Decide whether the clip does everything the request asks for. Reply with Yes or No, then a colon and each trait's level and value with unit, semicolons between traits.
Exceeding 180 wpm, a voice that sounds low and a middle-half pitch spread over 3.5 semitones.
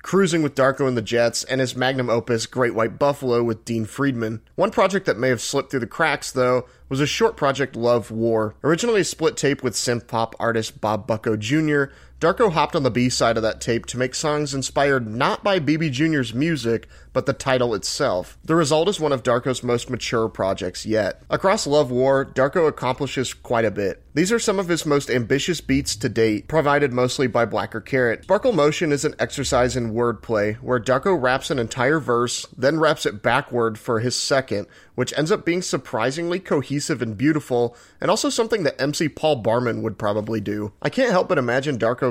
Yes: average, 200 wpm; low, 130 Hz; average, 4.2 semitones